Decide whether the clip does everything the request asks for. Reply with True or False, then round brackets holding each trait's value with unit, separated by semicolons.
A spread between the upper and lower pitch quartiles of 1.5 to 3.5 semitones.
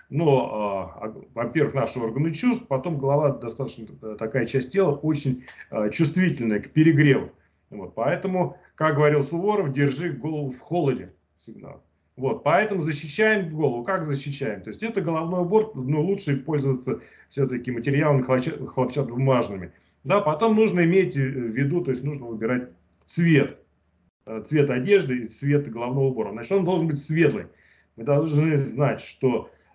False (4.4 semitones)